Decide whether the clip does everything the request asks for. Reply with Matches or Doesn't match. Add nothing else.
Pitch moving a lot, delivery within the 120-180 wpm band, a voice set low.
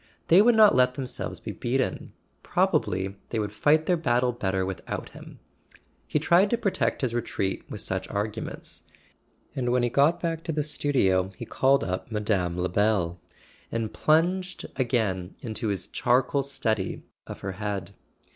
Matches